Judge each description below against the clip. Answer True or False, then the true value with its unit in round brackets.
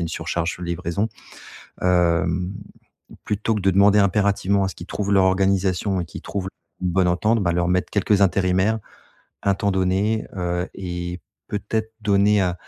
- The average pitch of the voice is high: False (95 Hz)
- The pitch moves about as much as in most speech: False (2.3 semitones)